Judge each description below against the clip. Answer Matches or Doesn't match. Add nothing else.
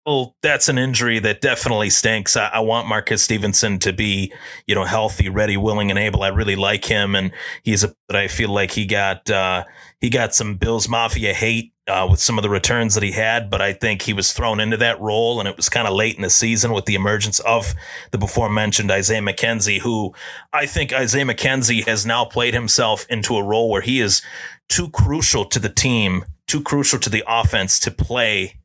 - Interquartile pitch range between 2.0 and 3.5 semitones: Matches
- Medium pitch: Doesn't match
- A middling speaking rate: Doesn't match